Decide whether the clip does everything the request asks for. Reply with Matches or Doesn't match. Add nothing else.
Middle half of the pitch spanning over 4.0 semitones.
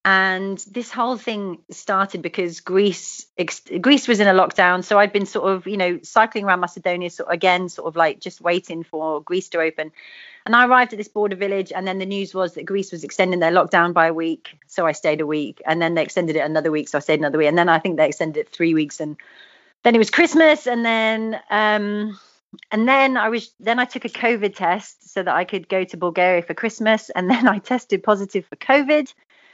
Matches